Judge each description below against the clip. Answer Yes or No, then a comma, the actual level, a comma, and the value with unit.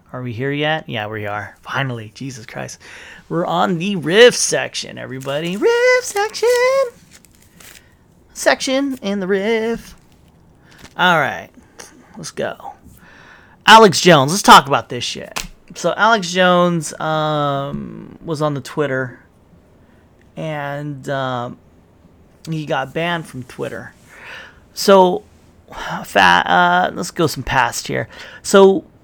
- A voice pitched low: No, medium, 155 Hz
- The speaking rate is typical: No, slow, 120 wpm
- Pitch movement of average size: No, wide, 7.3 semitones